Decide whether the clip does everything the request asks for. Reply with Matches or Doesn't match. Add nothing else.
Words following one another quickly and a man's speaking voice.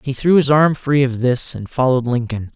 Matches